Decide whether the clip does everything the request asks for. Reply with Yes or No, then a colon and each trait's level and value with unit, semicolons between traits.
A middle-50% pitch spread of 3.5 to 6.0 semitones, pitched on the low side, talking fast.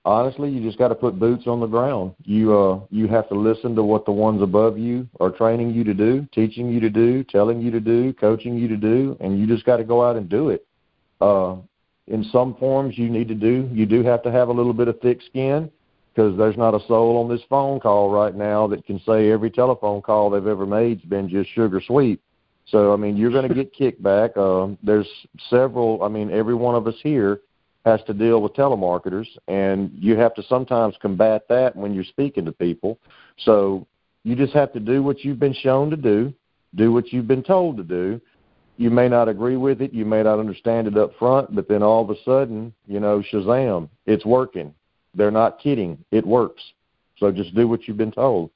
No: average, 2.8 semitones; low, 115 Hz; fast, 225 wpm